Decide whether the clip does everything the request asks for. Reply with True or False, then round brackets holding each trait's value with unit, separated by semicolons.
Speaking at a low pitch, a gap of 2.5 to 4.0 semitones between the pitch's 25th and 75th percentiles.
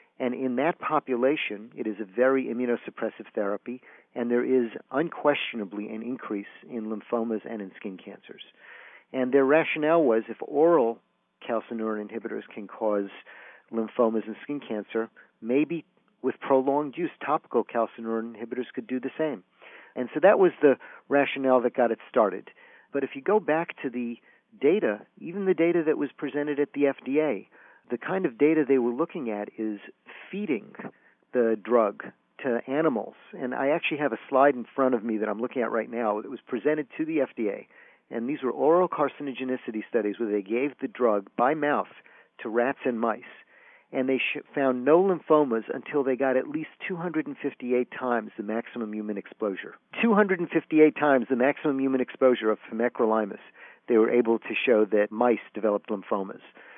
False (125 Hz; 4.4 semitones)